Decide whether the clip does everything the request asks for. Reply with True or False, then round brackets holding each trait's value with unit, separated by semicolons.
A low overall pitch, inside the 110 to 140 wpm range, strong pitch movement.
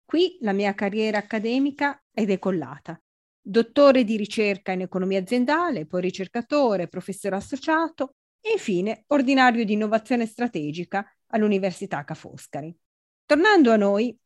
False (215 Hz; 120 wpm; 5.8 semitones)